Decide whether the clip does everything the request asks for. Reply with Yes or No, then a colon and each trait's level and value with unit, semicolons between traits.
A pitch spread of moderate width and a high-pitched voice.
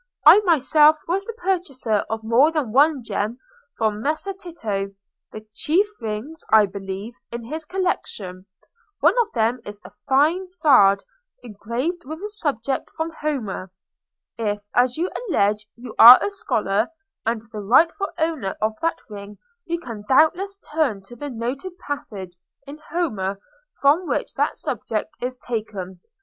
No: wide, 7.3 semitones; very high, 250 Hz